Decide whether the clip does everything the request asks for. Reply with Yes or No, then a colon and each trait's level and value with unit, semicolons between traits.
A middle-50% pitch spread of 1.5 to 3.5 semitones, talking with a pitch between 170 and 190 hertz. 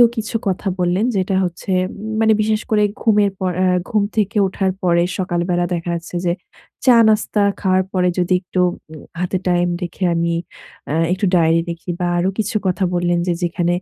Yes: average, 3.0 semitones; medium, 185 Hz